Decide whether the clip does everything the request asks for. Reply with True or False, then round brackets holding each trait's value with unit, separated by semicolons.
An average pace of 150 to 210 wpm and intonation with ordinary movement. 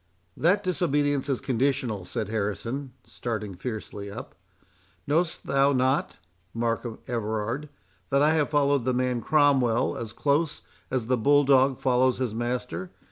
False (135 wpm; 3.7 semitones)